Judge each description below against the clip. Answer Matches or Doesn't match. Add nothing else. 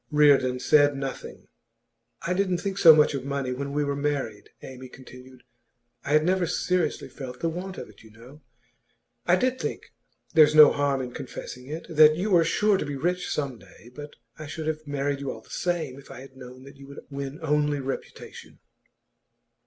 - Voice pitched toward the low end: Doesn't match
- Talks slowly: Doesn't match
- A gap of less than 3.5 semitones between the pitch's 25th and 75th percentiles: Matches